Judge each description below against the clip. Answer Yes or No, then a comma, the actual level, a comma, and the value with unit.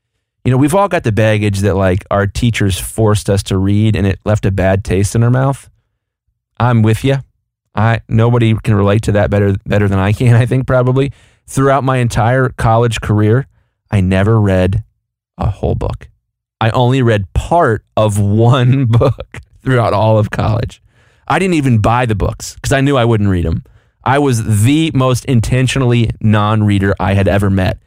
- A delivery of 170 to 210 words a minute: Yes, average, 185 wpm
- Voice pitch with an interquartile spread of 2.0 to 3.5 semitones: Yes, average, 3.2 semitones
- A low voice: Yes, low, 110 Hz